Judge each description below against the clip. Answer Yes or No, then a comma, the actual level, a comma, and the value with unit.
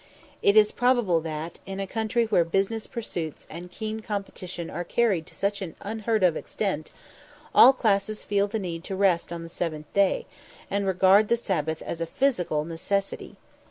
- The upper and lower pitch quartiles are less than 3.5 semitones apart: No, average, 4.2 semitones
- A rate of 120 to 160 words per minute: No, average, 175 wpm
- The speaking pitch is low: No, high, 195 Hz